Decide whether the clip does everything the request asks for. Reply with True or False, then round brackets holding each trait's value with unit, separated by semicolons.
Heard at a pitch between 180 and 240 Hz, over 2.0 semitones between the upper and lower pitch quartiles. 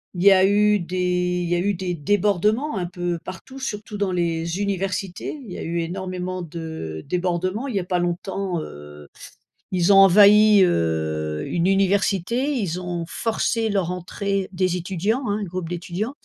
True (185 Hz; 2.7 semitones)